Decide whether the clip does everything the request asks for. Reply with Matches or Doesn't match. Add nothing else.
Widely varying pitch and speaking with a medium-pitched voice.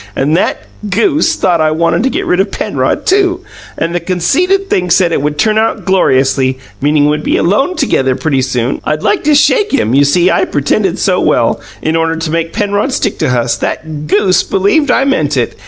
Matches